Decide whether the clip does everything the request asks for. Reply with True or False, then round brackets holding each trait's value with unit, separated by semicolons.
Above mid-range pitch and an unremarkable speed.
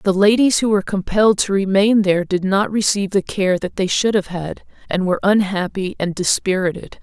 True (195 Hz; 195 wpm)